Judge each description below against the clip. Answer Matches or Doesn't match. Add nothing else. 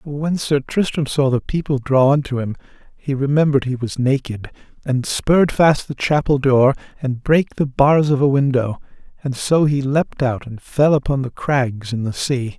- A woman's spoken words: Doesn't match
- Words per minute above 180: Matches